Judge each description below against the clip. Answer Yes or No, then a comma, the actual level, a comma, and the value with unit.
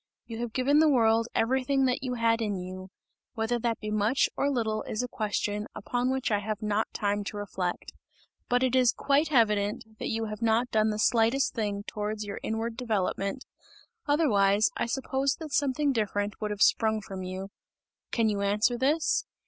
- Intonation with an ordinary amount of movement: Yes, average, 3.3 semitones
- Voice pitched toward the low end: No, high, 225 Hz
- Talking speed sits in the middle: Yes, average, 185 wpm